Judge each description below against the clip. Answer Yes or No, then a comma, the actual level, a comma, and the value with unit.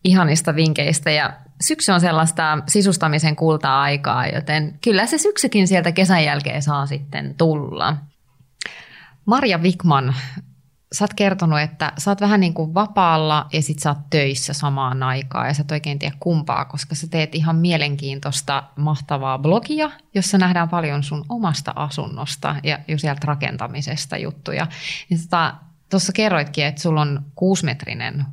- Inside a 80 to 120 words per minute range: No, average, 145 wpm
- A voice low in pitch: No, medium, 155 Hz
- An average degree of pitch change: Yes, average, 3.2 semitones